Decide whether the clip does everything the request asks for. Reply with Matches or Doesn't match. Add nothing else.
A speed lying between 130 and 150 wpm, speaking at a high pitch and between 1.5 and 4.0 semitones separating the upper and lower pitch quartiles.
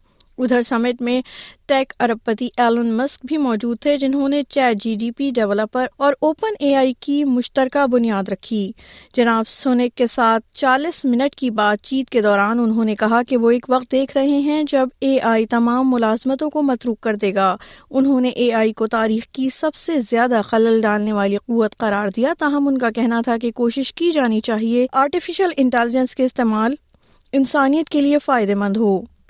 Doesn't match